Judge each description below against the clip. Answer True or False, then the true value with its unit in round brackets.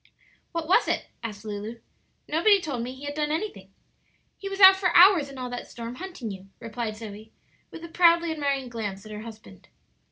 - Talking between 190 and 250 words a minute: True (195 wpm)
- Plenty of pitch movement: True (7.4 semitones)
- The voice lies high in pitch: True (260 Hz)